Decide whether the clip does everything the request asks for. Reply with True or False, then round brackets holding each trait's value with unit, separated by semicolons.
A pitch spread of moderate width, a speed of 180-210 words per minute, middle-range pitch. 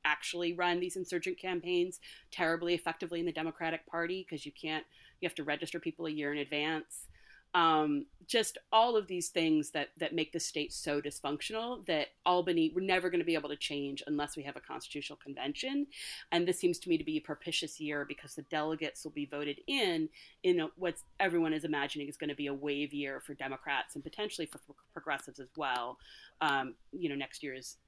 True (3.4 semitones; 200 wpm; 160 Hz)